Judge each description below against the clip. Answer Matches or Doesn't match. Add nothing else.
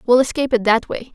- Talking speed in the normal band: Doesn't match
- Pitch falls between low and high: Doesn't match